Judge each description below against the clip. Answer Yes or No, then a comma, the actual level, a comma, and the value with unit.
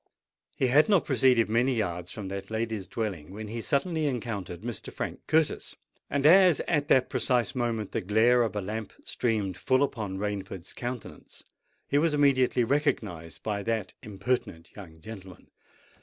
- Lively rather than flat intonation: No, average, 4.8 semitones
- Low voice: Yes, low, 115 Hz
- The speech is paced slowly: No, average, 155 wpm